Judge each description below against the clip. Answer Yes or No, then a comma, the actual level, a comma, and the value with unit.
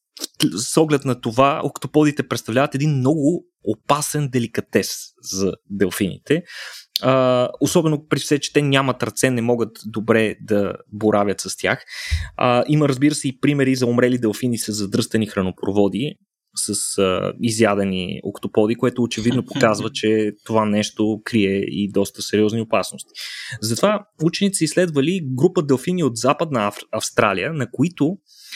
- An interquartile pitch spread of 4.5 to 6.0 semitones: Yes, average, 5.1 semitones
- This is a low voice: Yes, low, 125 Hz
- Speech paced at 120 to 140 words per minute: Yes, average, 130 wpm